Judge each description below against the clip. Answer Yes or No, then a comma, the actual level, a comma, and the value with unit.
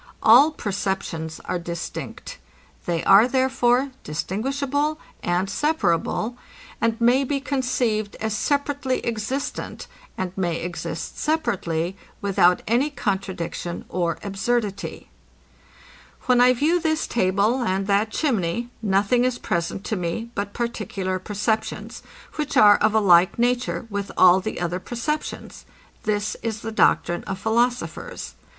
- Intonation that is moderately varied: Yes, average, 4.9 semitones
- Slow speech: Yes, slow, 125 wpm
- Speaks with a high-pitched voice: Yes, high, 215 Hz